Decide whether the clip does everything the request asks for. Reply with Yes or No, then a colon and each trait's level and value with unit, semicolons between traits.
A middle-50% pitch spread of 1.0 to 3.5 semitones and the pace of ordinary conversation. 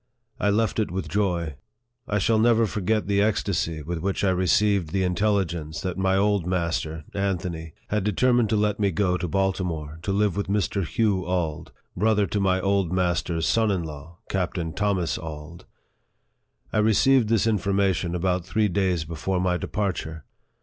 Yes: average, 3.2 semitones; average, 170 wpm